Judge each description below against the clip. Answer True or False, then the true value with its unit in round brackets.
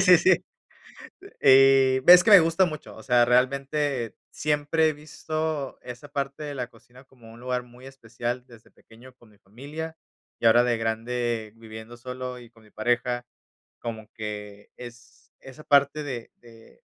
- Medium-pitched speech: False (125 Hz)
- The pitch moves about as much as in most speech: True (3.4 semitones)